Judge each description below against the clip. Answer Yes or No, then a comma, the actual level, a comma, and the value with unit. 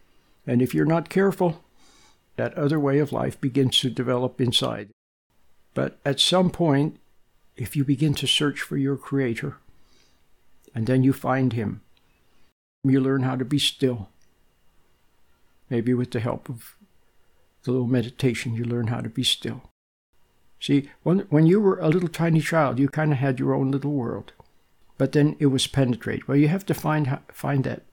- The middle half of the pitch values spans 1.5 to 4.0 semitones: Yes, average, 3.7 semitones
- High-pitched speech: No, low, 135 Hz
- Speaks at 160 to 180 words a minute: Yes, average, 175 wpm